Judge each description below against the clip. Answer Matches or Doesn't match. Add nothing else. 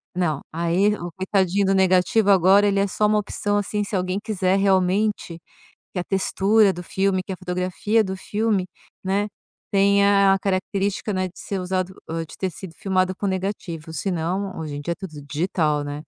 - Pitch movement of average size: Doesn't match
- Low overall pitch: Doesn't match